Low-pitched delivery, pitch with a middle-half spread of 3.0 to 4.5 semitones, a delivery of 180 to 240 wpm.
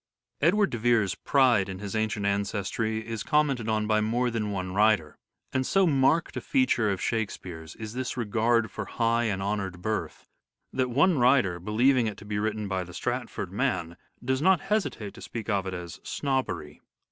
Yes: low, 110 Hz; average, 4.1 semitones; average, 190 wpm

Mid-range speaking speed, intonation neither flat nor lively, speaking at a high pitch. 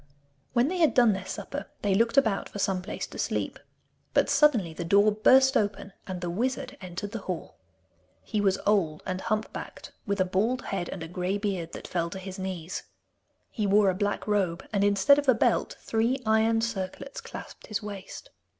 Yes: average, 195 wpm; average, 3.2 semitones; high, 205 Hz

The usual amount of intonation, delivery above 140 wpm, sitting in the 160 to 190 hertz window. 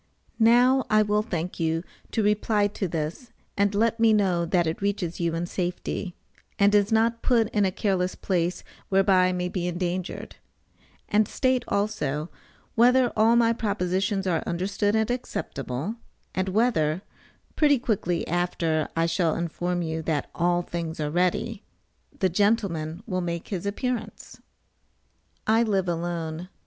Yes: average, 4.0 semitones; average, 150 wpm; medium, 185 Hz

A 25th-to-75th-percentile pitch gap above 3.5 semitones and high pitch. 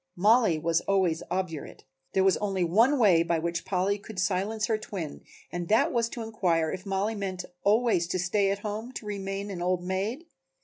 No: average, 3.2 semitones; high, 195 Hz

